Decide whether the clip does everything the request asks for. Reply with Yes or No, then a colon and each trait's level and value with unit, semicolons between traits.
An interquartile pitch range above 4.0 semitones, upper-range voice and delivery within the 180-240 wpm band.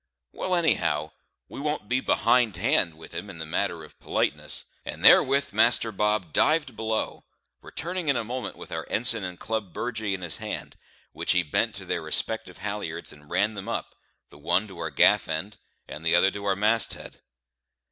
No: average, 5.1 semitones; low, 105 Hz; average, 190 wpm